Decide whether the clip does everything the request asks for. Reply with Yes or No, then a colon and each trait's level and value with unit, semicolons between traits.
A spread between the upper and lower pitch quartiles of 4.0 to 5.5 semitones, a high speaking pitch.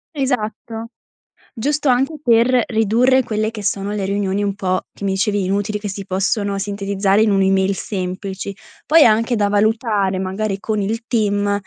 No: narrow, 2.4 semitones; high, 205 Hz